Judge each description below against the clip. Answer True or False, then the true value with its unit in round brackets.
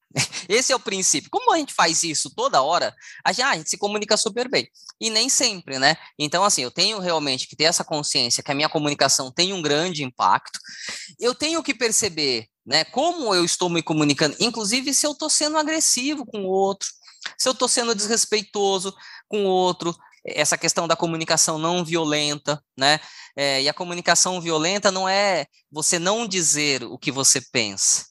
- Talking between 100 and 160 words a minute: False (185 wpm)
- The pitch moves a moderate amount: False (6.3 semitones)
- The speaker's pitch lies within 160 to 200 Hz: True (180 Hz)